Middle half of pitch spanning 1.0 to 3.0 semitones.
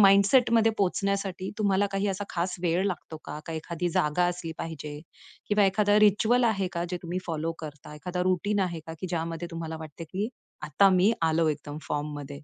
No: average, 3.6 semitones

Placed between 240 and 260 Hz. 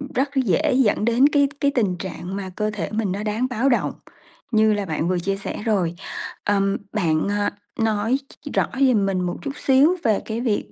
No: high, 215 Hz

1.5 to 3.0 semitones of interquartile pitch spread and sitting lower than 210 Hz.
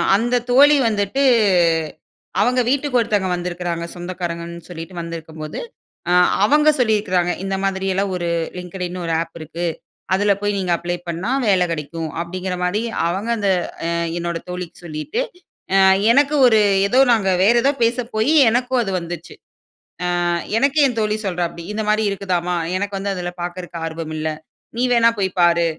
No: average, 4.1 semitones; medium, 185 Hz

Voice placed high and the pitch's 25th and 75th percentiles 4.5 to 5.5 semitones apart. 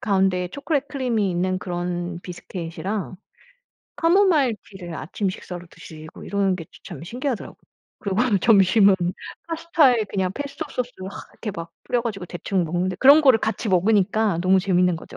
Yes: high, 195 Hz; average, 5.1 semitones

